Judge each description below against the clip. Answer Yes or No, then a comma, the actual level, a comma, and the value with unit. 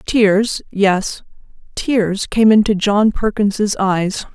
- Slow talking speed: Yes, slow, 85 wpm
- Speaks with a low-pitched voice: No, high, 205 Hz